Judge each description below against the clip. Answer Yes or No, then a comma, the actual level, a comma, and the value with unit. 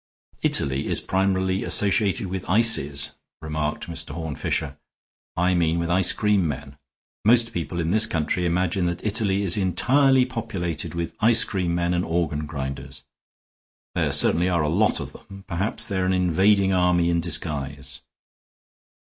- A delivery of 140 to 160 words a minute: Yes, average, 150 wpm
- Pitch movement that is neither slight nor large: Yes, average, 3.4 semitones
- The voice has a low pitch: Yes, very low, 90 Hz